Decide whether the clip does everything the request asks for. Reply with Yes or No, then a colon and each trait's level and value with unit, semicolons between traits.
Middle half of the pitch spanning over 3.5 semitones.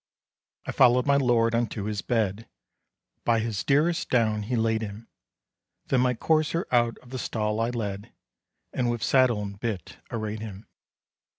No: average, 2.7 semitones